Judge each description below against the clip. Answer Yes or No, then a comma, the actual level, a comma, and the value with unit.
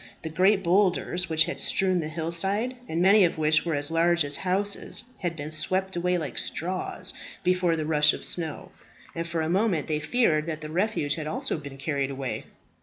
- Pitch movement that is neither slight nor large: Yes, average, 3.2 semitones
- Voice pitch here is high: No, medium, 165 Hz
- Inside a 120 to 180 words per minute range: No, average, 200 wpm